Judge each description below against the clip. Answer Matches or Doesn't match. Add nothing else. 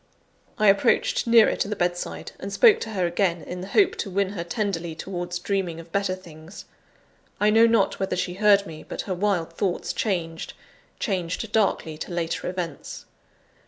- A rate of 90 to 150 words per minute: Doesn't match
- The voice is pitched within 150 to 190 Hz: Matches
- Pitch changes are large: Doesn't match